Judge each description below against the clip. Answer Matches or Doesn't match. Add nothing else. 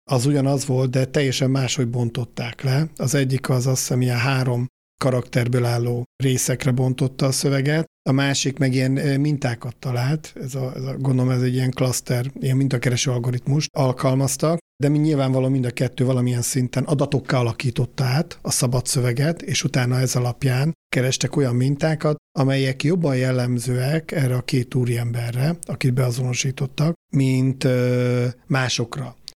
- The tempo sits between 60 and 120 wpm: Doesn't match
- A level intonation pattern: Matches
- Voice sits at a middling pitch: Doesn't match